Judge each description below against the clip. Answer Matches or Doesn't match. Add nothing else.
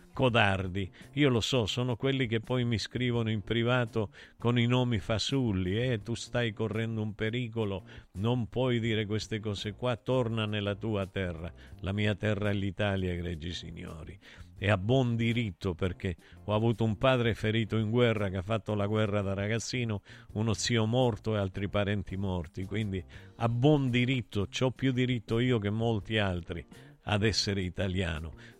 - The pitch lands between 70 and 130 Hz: Matches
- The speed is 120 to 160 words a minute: Doesn't match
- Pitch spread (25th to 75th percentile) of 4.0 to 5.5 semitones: Doesn't match